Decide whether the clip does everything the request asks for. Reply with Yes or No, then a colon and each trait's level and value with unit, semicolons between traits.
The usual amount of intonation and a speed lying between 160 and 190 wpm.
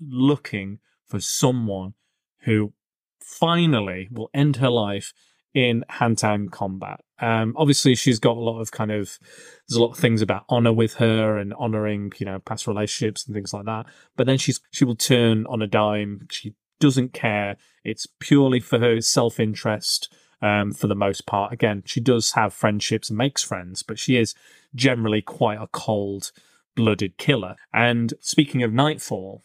Yes: average, 3.5 semitones; average, 165 wpm